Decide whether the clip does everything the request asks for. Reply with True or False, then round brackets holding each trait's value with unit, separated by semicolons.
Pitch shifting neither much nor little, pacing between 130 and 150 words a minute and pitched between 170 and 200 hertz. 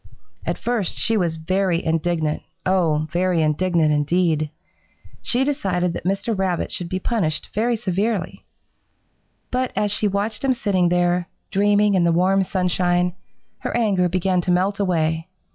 True (3.0 semitones; 145 wpm; 185 Hz)